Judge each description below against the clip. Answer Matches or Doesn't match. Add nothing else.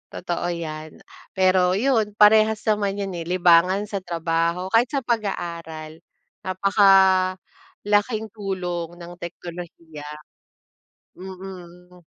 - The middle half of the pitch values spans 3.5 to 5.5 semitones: Doesn't match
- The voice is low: Doesn't match